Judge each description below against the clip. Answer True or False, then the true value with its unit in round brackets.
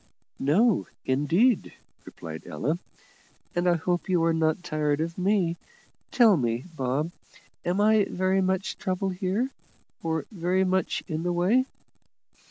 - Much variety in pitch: False (3.2 semitones)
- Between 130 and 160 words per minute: True (135 wpm)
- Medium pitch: True (175 Hz)